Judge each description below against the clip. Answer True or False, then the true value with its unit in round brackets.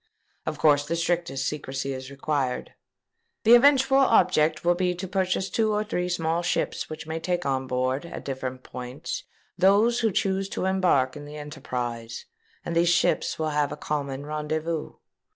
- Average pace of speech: True (170 wpm)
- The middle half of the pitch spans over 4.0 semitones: True (4.8 semitones)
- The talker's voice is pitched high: False (155 Hz)